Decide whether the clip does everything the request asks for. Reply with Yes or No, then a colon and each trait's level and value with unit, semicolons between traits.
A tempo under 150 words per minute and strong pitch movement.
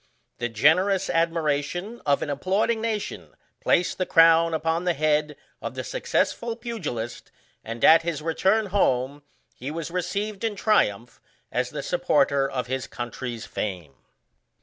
Yes: average, 140 wpm; wide, 6.0 semitones